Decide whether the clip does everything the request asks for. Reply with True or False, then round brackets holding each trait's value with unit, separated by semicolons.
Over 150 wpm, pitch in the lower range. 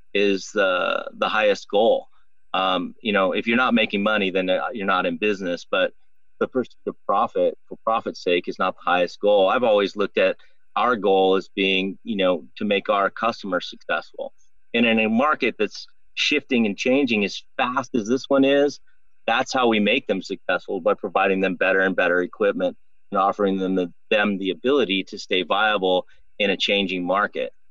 True (185 wpm; 105 Hz)